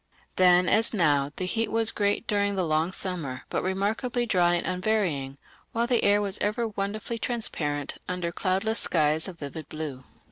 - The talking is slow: No, average, 170 wpm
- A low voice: No, medium, 185 Hz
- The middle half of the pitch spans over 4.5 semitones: Yes, average, 5.3 semitones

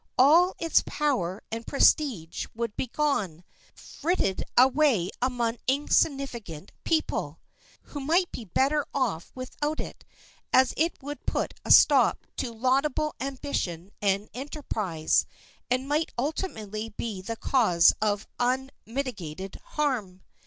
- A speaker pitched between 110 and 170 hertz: No, very high, 255 Hz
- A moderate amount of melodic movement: No, wide, 5.9 semitones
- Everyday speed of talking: No, slow, 115 wpm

